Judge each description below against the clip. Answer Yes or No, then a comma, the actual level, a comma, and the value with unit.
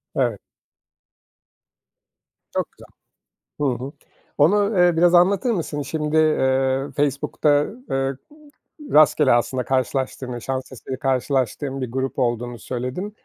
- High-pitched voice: No, low, 135 Hz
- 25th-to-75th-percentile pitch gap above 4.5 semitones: No, average, 3.2 semitones